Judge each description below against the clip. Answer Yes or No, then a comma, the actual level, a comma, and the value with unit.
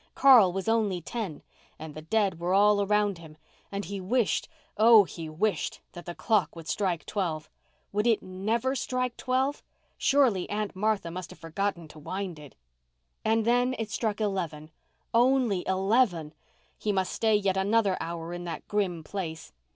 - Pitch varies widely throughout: No, average, 4.3 semitones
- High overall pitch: Yes, high, 195 Hz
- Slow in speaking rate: No, average, 160 wpm